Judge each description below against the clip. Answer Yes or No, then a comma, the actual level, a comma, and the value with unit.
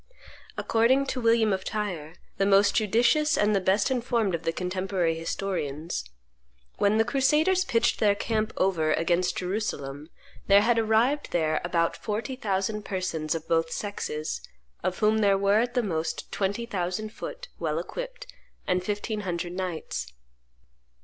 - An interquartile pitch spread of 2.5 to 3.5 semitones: No, average, 4.4 semitones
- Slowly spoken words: No, average, 150 wpm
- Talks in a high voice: Yes, high, 200 Hz